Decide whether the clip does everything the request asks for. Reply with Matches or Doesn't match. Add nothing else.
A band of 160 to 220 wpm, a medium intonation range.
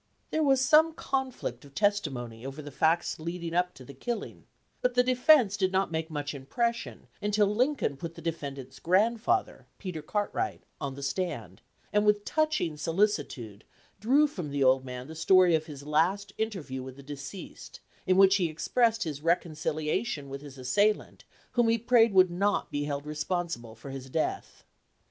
Doesn't match